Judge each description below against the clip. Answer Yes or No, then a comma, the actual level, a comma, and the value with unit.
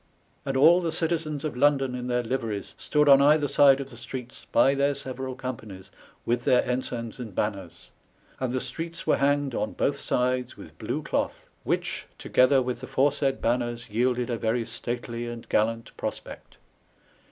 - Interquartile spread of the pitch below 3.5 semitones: Yes, average, 2.8 semitones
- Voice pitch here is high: No, low, 125 Hz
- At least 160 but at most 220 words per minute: Yes, average, 170 wpm